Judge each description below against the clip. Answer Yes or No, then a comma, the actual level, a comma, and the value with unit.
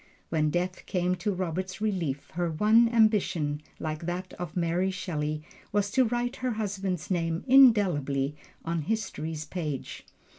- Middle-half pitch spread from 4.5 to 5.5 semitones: Yes, average, 4.9 semitones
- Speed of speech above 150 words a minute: No, average, 140 wpm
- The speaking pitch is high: No, medium, 180 Hz